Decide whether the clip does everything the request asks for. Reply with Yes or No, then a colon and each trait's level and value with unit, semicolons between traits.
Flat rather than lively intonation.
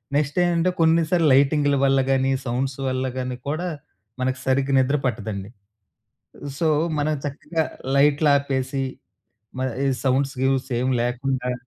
Yes: narrow, 2.3 semitones